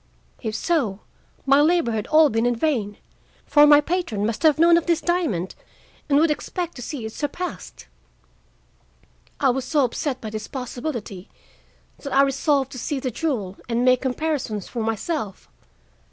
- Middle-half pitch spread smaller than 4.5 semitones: No, wide, 5.5 semitones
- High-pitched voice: Yes, very high, 270 Hz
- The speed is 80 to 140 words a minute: No, average, 165 wpm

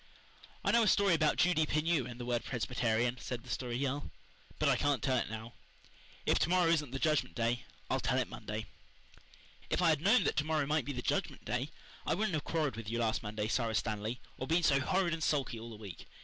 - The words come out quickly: Yes, fast, 235 wpm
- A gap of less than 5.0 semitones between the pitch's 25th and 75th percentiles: No, average, 5.3 semitones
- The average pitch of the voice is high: No, low, 135 Hz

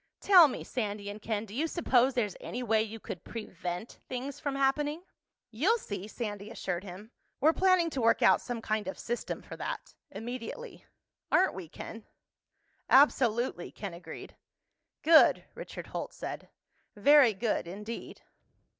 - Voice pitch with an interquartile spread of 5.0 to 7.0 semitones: Yes, average, 5.3 semitones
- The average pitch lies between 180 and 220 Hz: No, high, 230 Hz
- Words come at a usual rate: Yes, average, 145 wpm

